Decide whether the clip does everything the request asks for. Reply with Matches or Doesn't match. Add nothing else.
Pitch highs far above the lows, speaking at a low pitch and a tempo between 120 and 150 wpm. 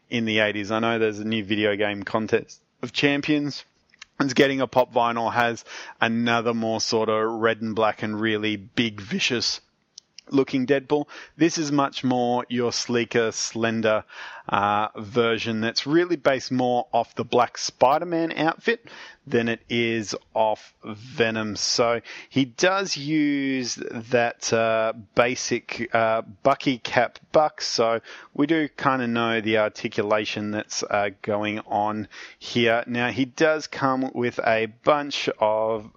Doesn't match